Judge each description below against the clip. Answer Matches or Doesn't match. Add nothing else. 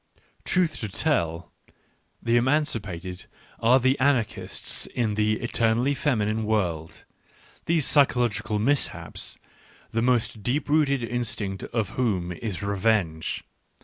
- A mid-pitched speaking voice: Doesn't match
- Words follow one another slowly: Matches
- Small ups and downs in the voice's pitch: Doesn't match